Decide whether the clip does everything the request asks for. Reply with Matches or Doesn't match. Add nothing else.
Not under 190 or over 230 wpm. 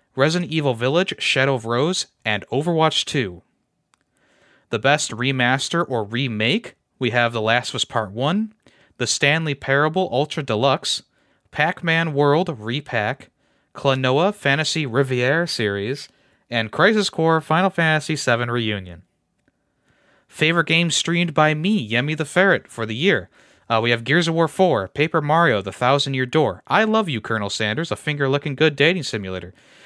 Doesn't match